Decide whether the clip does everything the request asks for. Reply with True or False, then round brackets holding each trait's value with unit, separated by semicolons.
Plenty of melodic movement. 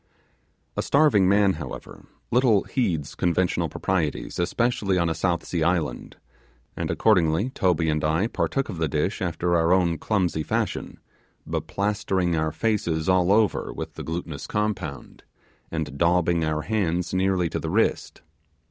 False (3.6 semitones)